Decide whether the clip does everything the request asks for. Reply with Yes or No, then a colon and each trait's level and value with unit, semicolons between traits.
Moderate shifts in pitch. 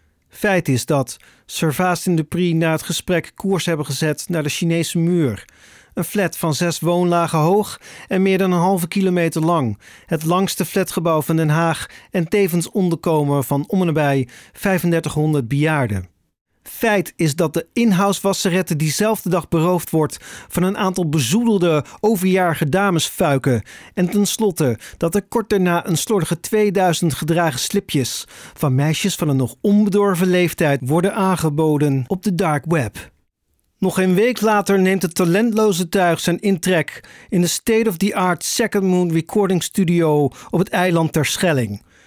Yes: average, 3.6 semitones